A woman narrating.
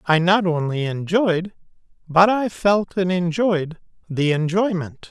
No: male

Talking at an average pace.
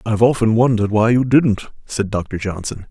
Yes: average, 185 wpm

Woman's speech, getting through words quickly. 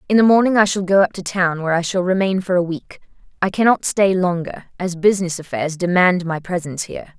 Yes: female; fast, 215 wpm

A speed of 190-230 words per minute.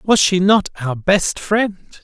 No: average, 175 wpm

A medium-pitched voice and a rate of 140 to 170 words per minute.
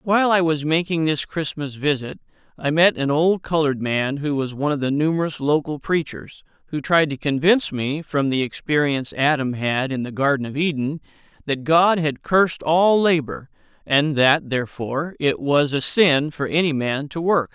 No: medium, 150 Hz; average, 185 wpm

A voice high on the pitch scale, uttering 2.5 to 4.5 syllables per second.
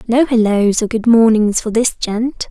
Yes: high, 225 Hz; 4.3 syllables/s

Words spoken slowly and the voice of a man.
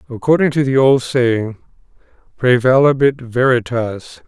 Yes: slow, 100 wpm; male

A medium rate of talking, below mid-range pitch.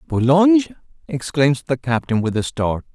No: average, 145 wpm; medium, 145 Hz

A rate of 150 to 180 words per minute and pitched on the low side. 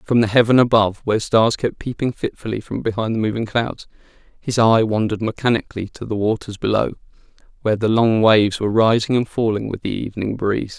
No: average, 190 wpm; low, 110 Hz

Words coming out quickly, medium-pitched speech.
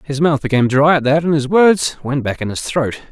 Yes: fast, 270 wpm; medium, 145 Hz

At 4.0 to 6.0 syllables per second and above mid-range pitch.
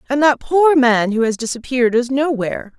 Yes: 5.5 syllables/s; very high, 255 Hz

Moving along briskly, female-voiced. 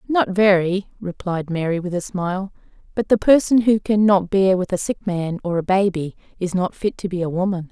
Yes: fast, 220 wpm; female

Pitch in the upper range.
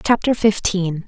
Yes: high, 200 Hz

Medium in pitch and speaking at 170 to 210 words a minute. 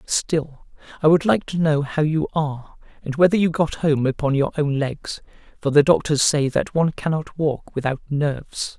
Yes: medium, 150 Hz; average, 190 wpm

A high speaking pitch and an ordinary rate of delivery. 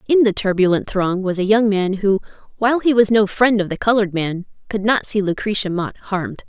No: high, 205 Hz; fast, 220 wpm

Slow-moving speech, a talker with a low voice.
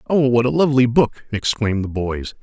No: average, 200 wpm; low, 120 Hz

